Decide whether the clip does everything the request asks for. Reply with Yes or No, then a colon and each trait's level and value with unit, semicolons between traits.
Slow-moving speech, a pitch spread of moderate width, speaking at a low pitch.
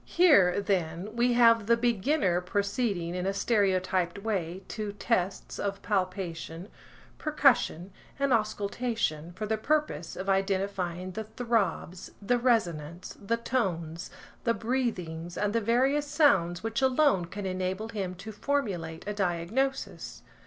No: slow, 130 wpm; average, 4.5 semitones; high, 200 Hz